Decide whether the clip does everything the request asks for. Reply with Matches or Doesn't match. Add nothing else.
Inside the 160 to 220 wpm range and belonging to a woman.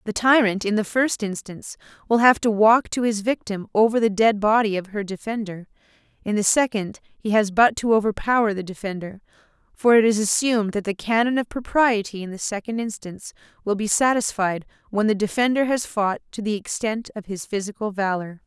Matches